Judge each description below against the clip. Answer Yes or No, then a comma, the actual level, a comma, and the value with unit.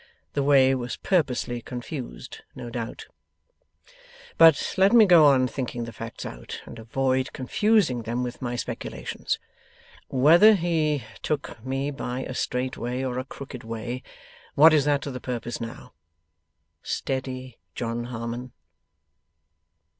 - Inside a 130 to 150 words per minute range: Yes, slow, 135 wpm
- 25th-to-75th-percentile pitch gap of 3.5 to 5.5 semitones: No, average, 3.0 semitones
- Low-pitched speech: Yes, low, 130 Hz